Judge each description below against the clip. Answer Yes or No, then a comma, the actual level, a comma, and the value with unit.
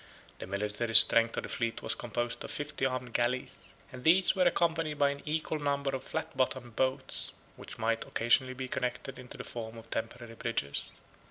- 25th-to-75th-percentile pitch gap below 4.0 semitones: Yes, average, 3.5 semitones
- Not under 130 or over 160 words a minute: No, average, 185 wpm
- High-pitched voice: No, low, 125 Hz